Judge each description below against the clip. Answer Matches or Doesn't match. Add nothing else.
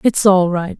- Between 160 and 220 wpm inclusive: Doesn't match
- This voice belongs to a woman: Matches